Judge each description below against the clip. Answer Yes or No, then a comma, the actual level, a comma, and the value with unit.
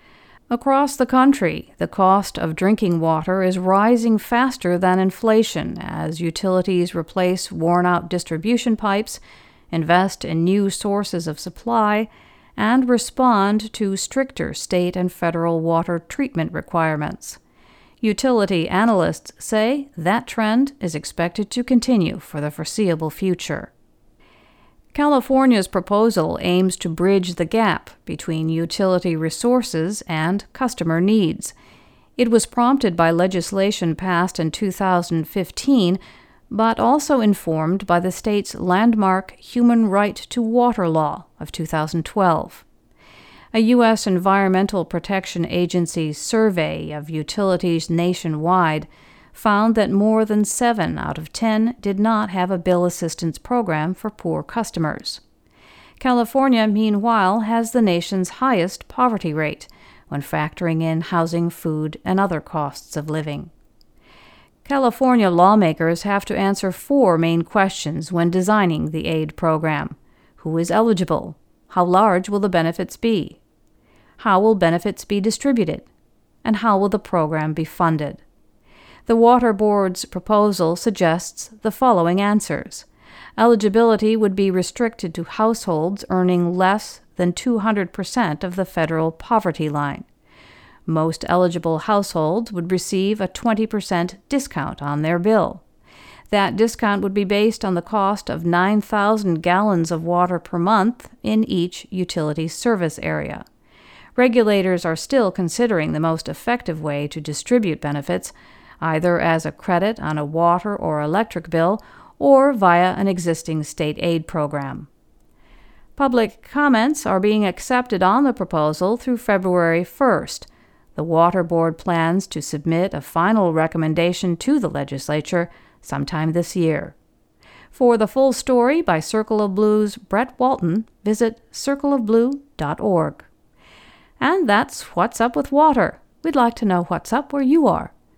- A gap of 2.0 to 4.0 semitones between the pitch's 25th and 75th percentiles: No, average, 4.8 semitones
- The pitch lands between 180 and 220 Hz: Yes, high, 190 Hz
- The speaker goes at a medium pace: No, slow, 130 wpm